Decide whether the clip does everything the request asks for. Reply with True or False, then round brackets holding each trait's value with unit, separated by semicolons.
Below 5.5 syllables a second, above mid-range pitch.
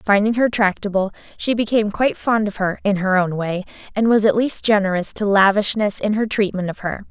False (5.7 syllables/s; 205 Hz)